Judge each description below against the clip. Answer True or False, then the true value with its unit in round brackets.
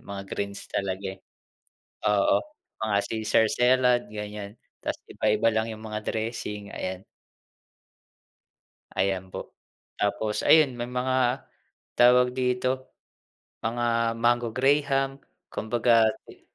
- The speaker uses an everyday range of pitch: True (3.1 semitones)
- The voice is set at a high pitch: False (115 Hz)